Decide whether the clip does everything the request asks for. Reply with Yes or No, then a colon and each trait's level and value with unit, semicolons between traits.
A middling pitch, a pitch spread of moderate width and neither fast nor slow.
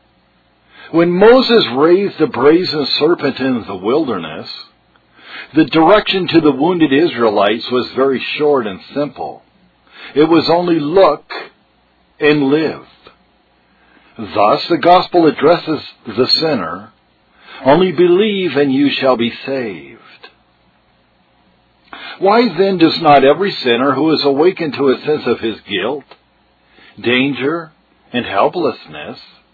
No: medium, 145 Hz; average, 5.0 semitones; slow, 115 wpm